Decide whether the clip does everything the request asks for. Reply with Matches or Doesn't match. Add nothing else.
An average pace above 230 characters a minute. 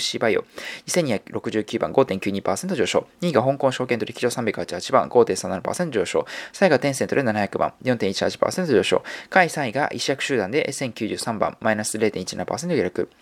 Doesn't match